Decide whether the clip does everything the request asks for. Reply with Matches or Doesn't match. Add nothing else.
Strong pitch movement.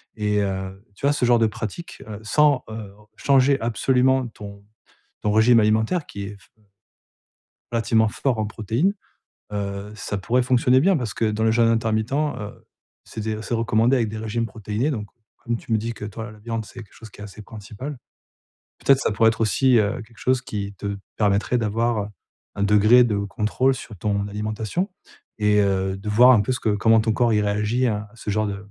Doesn't match